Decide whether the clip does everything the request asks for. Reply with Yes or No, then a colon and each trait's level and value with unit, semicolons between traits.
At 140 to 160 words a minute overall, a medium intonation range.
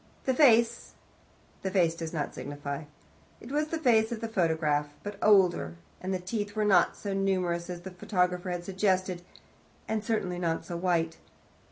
No: average, 170 wpm; average, 3.7 semitones